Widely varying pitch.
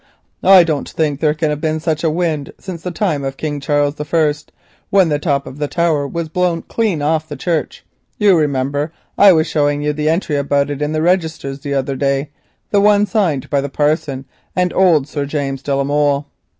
No: average, 2.8 semitones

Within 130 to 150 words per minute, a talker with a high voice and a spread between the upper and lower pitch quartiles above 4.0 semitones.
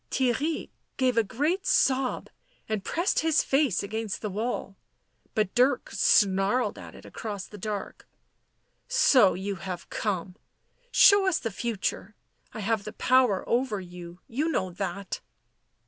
Yes: average, 145 wpm; high, 220 Hz; average, 5.0 semitones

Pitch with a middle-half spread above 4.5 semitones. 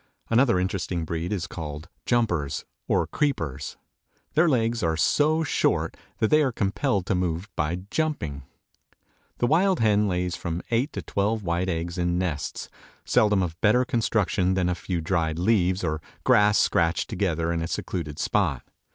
Yes: average, 5.2 semitones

